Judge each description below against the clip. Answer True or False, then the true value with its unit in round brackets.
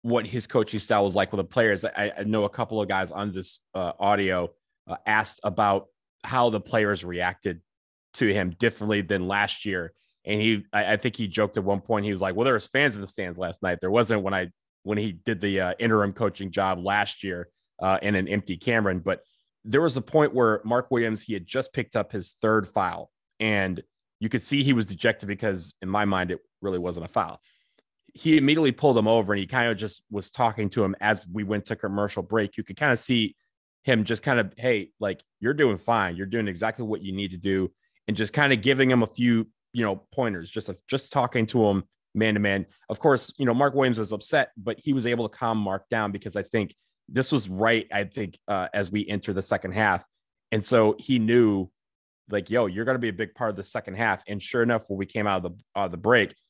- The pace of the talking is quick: True (240 wpm)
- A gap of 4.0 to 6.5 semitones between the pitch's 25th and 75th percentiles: False (3.0 semitones)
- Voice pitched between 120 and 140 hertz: False (105 Hz)